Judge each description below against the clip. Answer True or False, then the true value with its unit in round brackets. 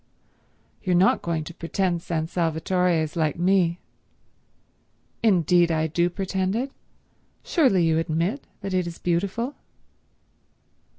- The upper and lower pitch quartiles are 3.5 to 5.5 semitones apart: False (2.5 semitones)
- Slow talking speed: True (120 wpm)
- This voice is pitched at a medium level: True (175 Hz)